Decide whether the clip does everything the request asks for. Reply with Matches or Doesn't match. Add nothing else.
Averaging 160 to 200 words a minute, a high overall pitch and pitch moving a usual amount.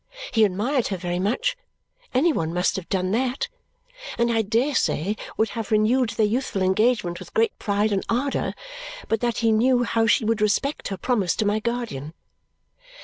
Matches